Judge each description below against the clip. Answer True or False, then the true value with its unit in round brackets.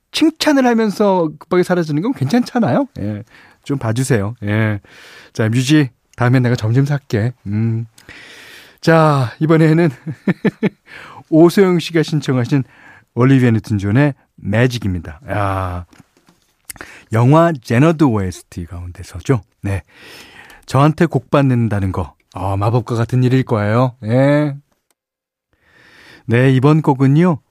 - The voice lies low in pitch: True (130 Hz)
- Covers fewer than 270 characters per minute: True (240 characters per minute)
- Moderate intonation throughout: False (5.9 semitones)